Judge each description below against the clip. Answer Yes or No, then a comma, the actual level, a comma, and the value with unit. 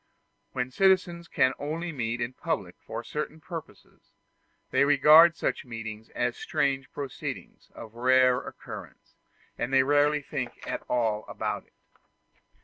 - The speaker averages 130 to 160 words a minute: Yes, average, 140 wpm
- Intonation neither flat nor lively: Yes, average, 3.8 semitones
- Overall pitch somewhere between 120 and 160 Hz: Yes, low, 135 Hz